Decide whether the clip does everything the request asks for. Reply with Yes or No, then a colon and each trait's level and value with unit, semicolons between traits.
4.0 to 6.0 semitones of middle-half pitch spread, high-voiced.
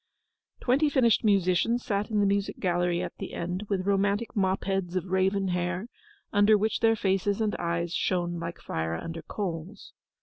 No: average, 2.8 semitones; high, 195 Hz